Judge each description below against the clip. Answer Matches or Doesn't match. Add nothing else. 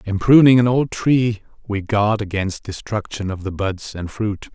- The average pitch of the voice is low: Matches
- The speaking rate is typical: Matches